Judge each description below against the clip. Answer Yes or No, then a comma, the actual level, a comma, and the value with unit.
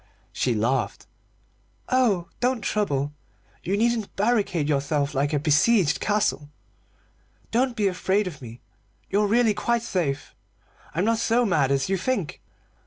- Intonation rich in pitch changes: Yes, wide, 7.7 semitones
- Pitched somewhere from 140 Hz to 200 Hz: Yes, high, 190 Hz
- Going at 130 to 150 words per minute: Yes, slow, 135 wpm